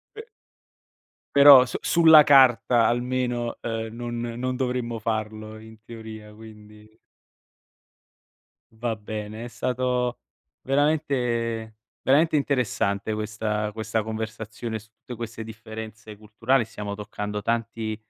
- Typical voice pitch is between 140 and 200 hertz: No, low, 115 Hz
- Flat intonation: Yes, narrow, 2.3 semitones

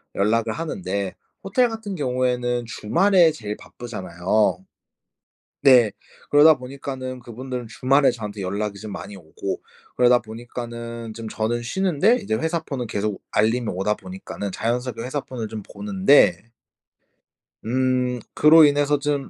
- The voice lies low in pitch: Yes, low, 125 Hz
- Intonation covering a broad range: No, average, 4.8 semitones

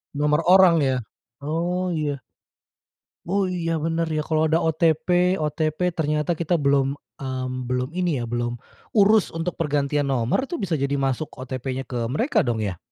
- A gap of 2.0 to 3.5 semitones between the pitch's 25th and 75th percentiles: No, average, 4.0 semitones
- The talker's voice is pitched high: No, medium, 155 Hz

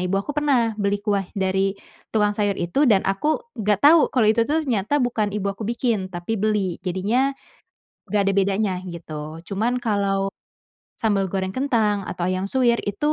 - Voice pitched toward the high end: Yes, high, 205 Hz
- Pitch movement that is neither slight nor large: Yes, average, 3.1 semitones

